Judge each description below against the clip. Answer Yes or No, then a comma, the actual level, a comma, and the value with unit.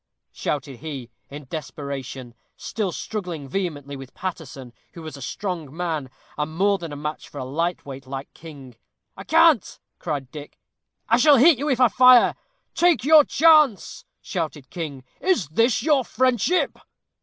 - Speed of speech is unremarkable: Yes, average, 155 wpm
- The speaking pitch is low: No, medium, 160 Hz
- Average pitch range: No, wide, 8.8 semitones